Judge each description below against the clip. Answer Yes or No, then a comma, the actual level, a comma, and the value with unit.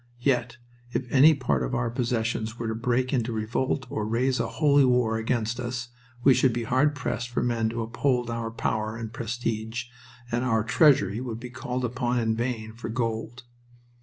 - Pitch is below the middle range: Yes, low, 120 Hz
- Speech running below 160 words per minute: No, average, 185 wpm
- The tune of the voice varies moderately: No, narrow, 2.0 semitones